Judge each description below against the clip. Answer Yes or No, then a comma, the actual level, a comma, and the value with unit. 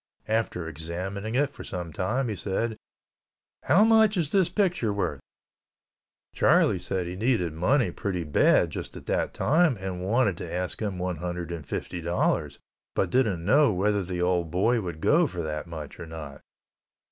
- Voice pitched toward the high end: No, very low, 95 Hz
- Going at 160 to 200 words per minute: Yes, average, 170 wpm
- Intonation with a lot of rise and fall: Yes, wide, 5.8 semitones